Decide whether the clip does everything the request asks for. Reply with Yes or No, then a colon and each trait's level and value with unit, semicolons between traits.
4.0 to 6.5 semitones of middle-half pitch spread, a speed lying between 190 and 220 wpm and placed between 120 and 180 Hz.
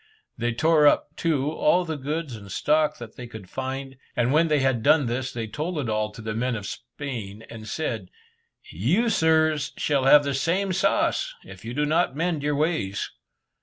Yes: average, 5.1 semitones; average, 195 wpm; medium, 140 Hz